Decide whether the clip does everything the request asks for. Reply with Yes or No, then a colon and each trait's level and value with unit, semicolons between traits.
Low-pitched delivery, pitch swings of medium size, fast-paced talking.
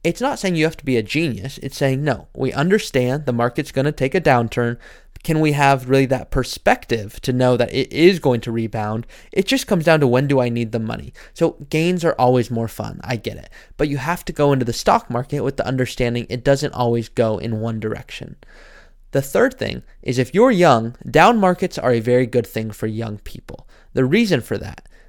Yes: low, 130 Hz; average, 5.0 semitones; fast, 225 wpm